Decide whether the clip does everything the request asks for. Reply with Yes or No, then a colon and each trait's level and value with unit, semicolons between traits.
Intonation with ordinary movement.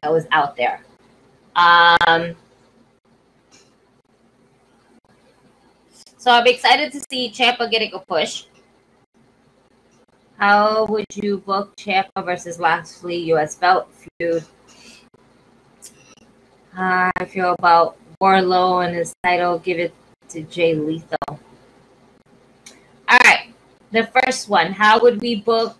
Yes: average, 4.2 semitones